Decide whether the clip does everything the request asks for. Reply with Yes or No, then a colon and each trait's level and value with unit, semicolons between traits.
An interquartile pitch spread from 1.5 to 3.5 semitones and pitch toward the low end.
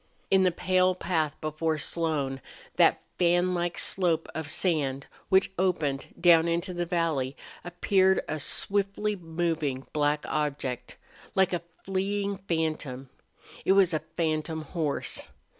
No: average, 3.2 semitones; medium, 170 Hz